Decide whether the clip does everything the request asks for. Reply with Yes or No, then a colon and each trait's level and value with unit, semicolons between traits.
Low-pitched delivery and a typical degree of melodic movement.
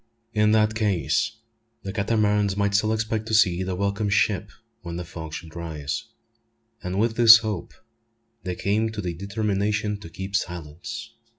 Yes: low, 100 Hz; average, 3.5 semitones